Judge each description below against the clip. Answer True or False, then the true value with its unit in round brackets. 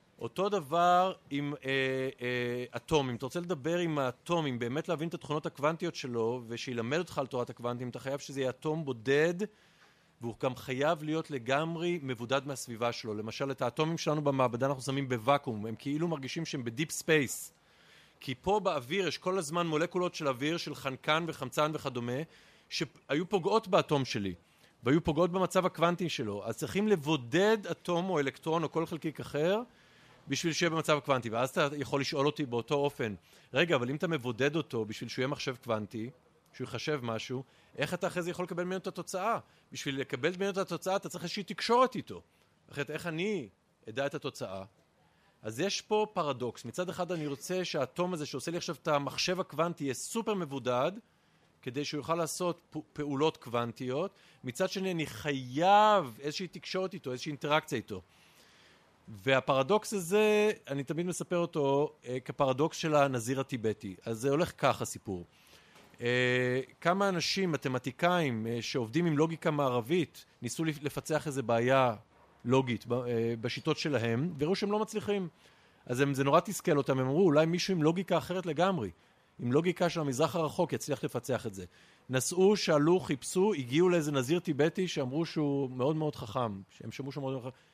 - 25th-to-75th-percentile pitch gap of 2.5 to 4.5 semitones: False (5.0 semitones)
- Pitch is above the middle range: False (150 Hz)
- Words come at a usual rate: False (165 wpm)